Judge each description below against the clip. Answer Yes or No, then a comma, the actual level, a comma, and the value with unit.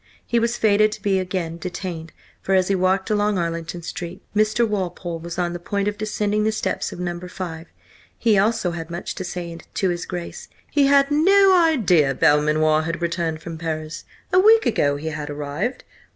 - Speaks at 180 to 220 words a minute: Yes, average, 195 wpm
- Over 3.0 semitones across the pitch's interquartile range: Yes, average, 4.2 semitones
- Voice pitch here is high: No, medium, 180 Hz